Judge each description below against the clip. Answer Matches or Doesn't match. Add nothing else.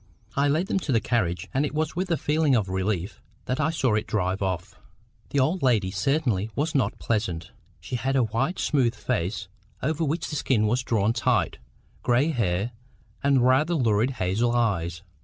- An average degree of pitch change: Doesn't match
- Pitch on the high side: Doesn't match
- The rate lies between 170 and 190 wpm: Matches